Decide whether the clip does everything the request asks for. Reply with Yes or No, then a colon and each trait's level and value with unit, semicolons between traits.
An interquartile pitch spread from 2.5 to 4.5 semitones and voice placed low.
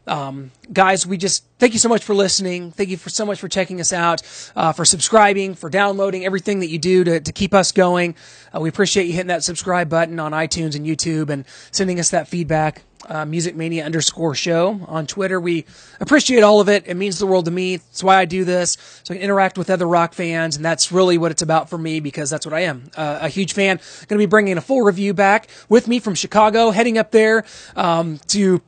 No: average, 3.2 semitones; medium, 180 Hz